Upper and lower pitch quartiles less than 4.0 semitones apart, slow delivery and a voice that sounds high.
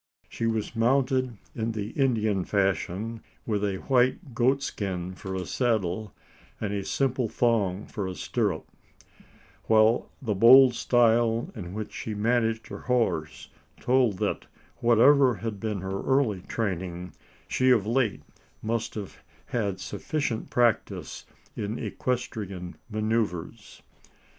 No: average, 3.6 semitones; slow, 125 wpm; low, 110 Hz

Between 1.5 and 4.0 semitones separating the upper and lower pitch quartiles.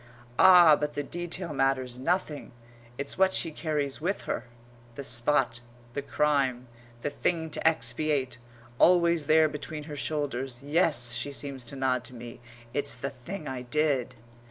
Yes: average, 3.5 semitones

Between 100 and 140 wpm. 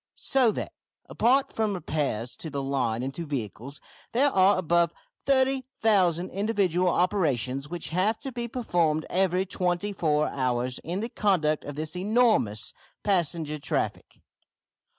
Yes: slow, 135 wpm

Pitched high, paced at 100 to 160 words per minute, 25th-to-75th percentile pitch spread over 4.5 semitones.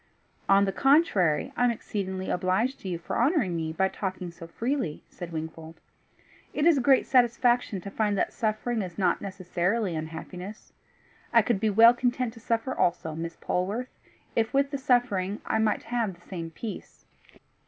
No: high, 200 Hz; average, 175 wpm; average, 5.3 semitones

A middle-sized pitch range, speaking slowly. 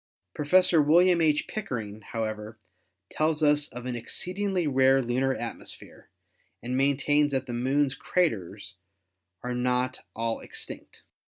Yes: average, 3.9 semitones; slow, 125 wpm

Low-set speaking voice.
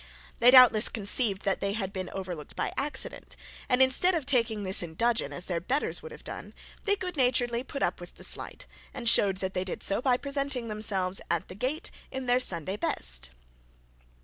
No: high, 230 Hz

